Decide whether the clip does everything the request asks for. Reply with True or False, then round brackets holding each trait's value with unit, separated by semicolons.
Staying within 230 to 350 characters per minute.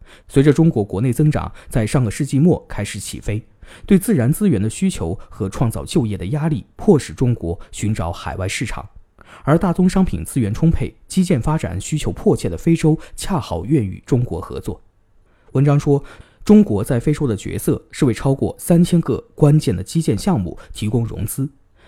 True (275 characters per minute)